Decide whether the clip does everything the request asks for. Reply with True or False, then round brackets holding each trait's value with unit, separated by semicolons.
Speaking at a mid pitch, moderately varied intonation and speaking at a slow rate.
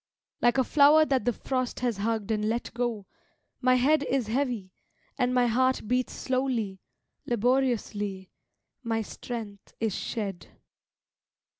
False (240 Hz; 3.2 semitones; 130 wpm)